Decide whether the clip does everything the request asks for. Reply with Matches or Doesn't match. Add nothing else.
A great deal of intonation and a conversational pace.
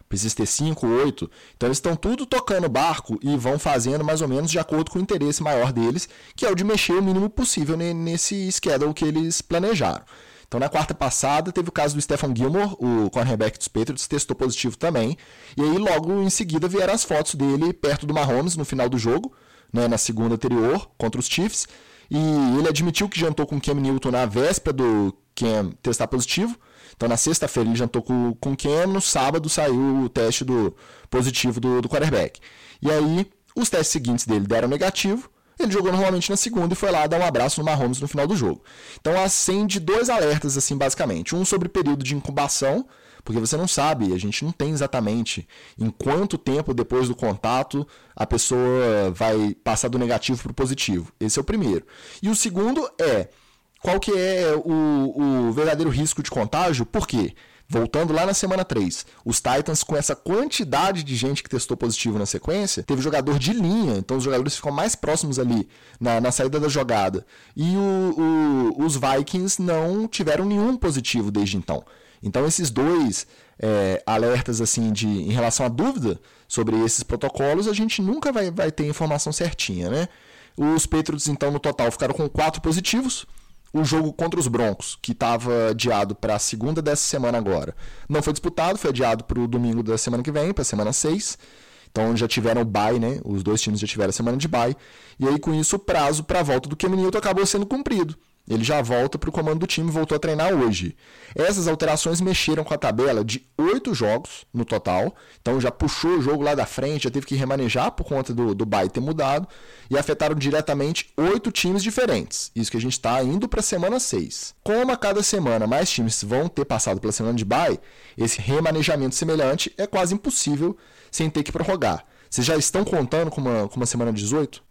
Doesn't match